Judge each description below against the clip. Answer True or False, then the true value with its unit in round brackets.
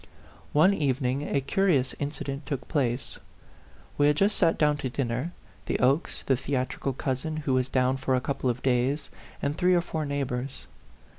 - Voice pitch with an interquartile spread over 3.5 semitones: False (2.6 semitones)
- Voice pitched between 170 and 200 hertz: False (140 Hz)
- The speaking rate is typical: True (170 wpm)